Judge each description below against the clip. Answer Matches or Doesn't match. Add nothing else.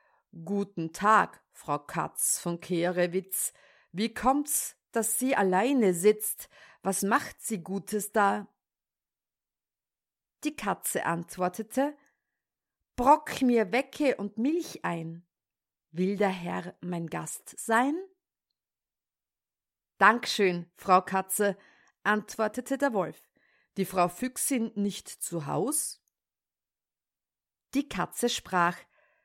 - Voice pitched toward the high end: Matches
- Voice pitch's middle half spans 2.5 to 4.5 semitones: Doesn't match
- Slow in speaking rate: Matches